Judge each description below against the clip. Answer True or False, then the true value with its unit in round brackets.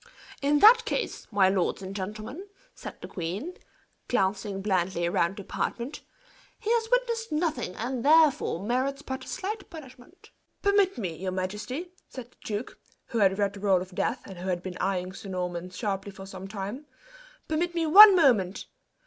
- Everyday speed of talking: True (170 wpm)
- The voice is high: True (210 Hz)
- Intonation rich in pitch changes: True (8.4 semitones)